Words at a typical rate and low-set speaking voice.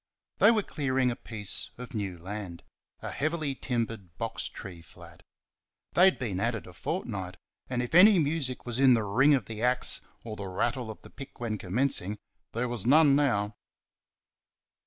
Yes: average, 180 wpm; low, 120 Hz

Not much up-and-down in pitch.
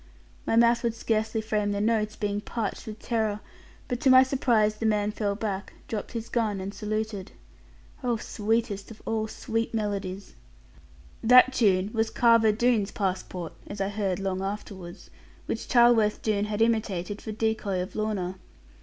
Yes: narrow, 2.0 semitones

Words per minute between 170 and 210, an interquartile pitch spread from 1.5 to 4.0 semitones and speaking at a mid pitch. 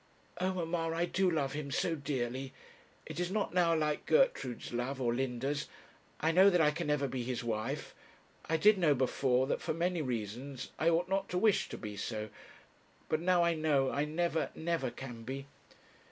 No: average, 190 wpm; average, 4.8 semitones; medium, 150 Hz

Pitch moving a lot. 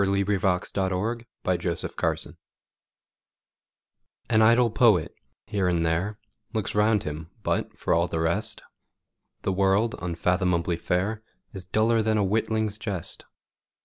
No: average, 3.5 semitones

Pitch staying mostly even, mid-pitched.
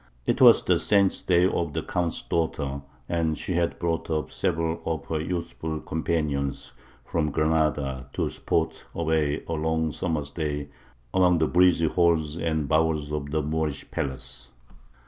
No: narrow, 2.0 semitones; very low, 80 Hz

